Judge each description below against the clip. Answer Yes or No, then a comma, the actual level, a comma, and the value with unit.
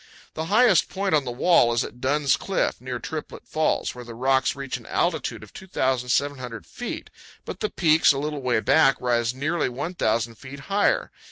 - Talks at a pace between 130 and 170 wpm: No, average, 180 wpm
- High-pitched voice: No, low, 135 Hz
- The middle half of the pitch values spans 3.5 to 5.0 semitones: Yes, average, 4.4 semitones